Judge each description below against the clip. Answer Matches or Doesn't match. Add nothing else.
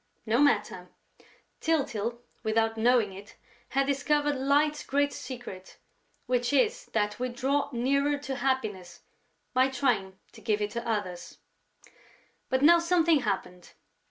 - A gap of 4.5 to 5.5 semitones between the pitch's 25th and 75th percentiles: Matches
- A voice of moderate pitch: Doesn't match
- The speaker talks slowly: Matches